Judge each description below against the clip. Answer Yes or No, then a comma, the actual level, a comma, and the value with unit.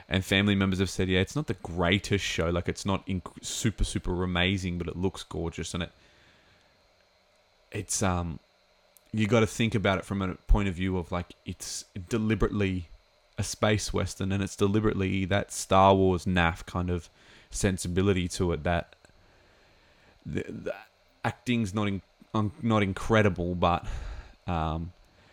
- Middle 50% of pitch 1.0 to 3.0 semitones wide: Yes, narrow, 2.6 semitones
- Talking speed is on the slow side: No, average, 160 wpm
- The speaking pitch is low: Yes, very low, 95 Hz